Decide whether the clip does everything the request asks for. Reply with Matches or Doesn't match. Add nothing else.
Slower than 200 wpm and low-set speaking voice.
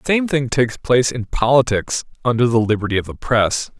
Doesn't match